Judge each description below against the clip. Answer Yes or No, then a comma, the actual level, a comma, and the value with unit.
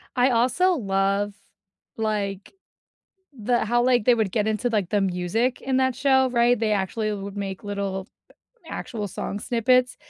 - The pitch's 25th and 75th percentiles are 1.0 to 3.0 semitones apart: No, average, 3.6 semitones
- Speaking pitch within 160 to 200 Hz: No, high, 220 Hz